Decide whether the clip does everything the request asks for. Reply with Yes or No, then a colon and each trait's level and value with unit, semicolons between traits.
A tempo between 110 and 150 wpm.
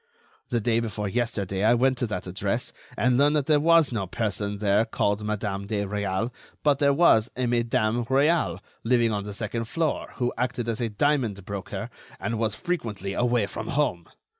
No: average, 185 wpm